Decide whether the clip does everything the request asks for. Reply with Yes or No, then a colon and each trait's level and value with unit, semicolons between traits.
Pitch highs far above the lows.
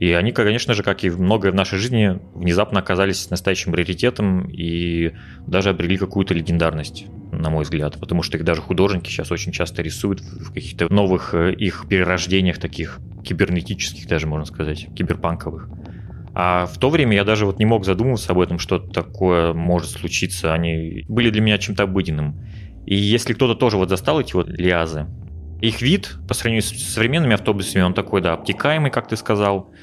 No: average, 3.4 semitones